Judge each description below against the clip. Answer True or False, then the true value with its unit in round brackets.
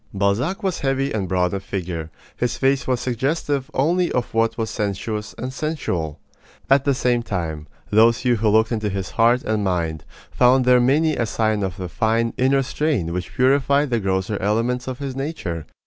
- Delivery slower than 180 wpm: False (185 wpm)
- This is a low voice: True (115 Hz)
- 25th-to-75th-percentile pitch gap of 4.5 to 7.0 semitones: True (5.2 semitones)